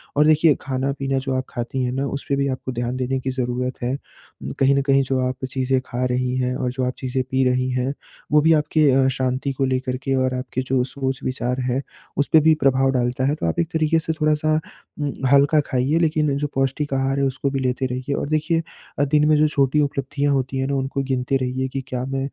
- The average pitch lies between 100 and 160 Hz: Yes, low, 135 Hz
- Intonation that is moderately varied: No, narrow, 1.7 semitones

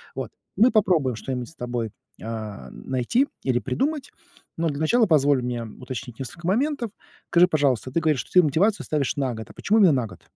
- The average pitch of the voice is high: No, medium, 145 Hz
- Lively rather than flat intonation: Yes, wide, 6.8 semitones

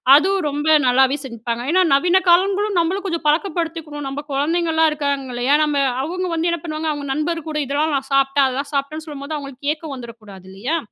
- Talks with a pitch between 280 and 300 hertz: Yes, very high, 295 Hz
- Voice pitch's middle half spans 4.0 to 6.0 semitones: No, average, 3.4 semitones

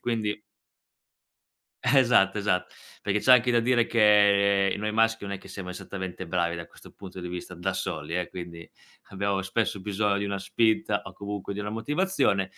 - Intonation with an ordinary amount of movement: Yes, average, 3.0 semitones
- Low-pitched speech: Yes, low, 100 Hz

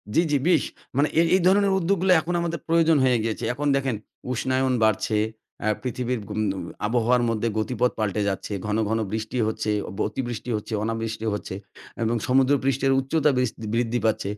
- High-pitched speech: No, low, 125 Hz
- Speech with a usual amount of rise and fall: Yes, average, 4.0 semitones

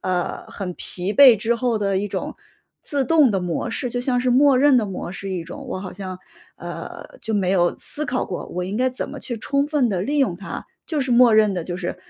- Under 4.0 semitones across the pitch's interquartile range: No, wide, 5.4 semitones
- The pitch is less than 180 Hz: No, high, 220 Hz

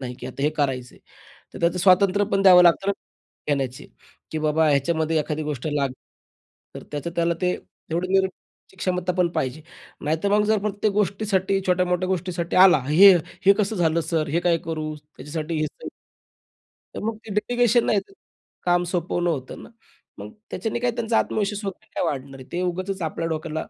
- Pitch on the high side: No, medium, 175 Hz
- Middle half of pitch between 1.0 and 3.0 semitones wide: No, average, 4.2 semitones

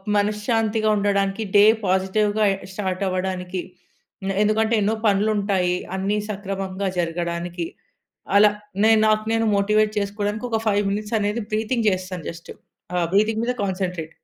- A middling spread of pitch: No, narrow, 2.3 semitones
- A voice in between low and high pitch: No, high, 200 Hz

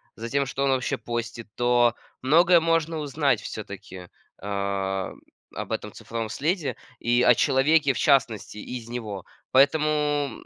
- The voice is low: Yes, low, 125 Hz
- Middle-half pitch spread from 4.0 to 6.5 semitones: Yes, average, 4.7 semitones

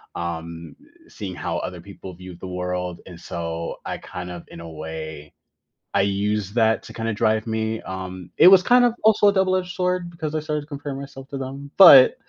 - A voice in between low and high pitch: No, low, 110 Hz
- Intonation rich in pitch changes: Yes, wide, 8.9 semitones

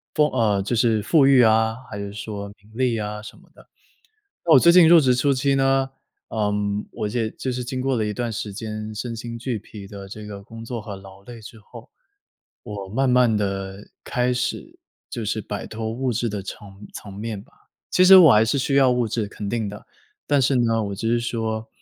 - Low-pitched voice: Yes, low, 115 Hz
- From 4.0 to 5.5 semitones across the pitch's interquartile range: No, average, 3.3 semitones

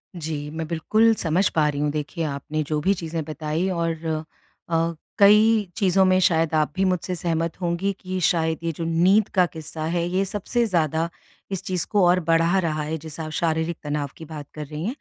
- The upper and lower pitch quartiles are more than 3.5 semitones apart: No, average, 2.9 semitones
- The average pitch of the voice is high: No, medium, 165 Hz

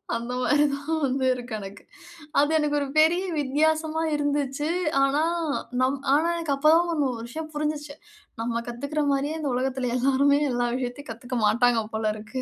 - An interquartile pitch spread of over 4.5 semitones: No, average, 3.5 semitones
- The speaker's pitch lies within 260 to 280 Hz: Yes, very high, 275 Hz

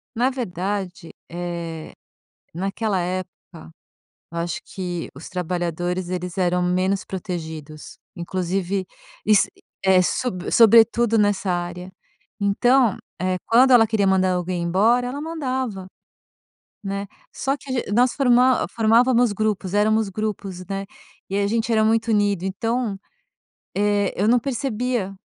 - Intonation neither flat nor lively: Yes, average, 4.0 semitones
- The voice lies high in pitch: Yes, high, 200 Hz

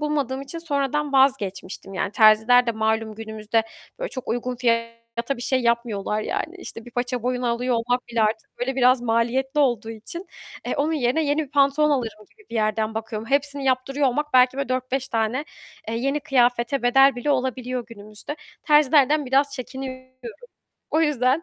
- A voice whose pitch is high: Yes, very high, 250 Hz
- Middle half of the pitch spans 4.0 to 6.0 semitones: No, average, 3.2 semitones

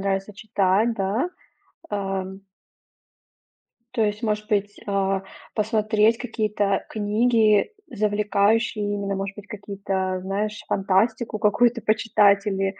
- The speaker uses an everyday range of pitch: No, narrow, 1.7 semitones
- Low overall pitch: No, high, 205 Hz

